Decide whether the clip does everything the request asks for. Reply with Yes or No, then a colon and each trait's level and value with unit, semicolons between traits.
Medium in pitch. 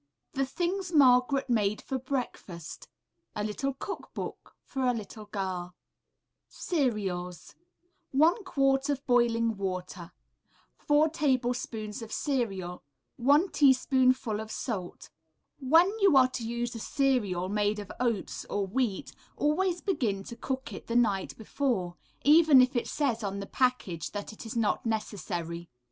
No: high, 240 Hz